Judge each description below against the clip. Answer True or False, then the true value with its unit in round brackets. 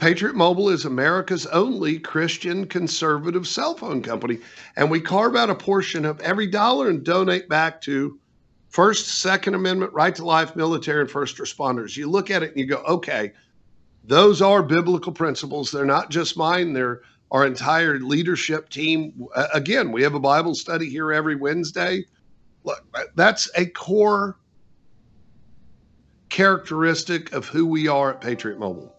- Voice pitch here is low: False (165 Hz)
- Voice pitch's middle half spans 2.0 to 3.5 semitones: False (3.9 semitones)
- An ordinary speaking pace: True (155 wpm)